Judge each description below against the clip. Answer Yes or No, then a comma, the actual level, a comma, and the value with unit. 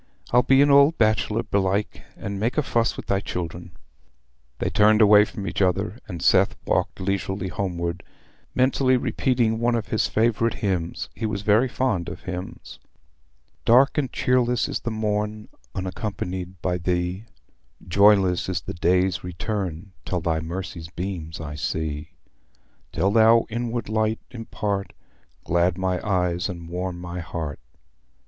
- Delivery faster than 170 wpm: No, average, 145 wpm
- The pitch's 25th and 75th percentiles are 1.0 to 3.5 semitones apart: No, average, 3.9 semitones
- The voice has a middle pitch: No, low, 100 Hz